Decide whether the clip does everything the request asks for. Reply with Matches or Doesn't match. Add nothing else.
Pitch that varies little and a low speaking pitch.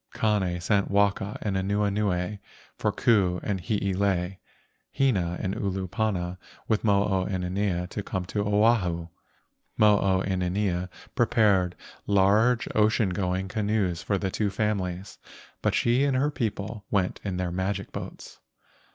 Matches